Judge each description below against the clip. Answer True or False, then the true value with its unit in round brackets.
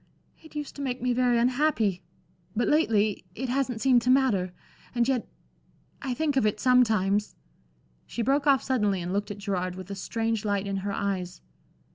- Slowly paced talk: False (180 wpm)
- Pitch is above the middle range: True (225 Hz)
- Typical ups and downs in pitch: True (4.4 semitones)